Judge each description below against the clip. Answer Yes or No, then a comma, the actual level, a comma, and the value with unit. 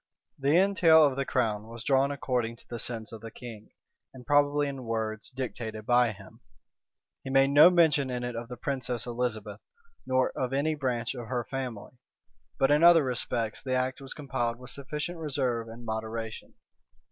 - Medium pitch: No, low, 125 Hz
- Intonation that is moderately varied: Yes, average, 3.3 semitones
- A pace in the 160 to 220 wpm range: Yes, average, 180 wpm